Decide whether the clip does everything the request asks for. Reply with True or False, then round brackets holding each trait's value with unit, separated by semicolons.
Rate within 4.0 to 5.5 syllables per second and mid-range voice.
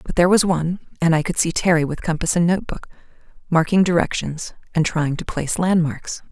False (6.1 syllables/s; 170 Hz)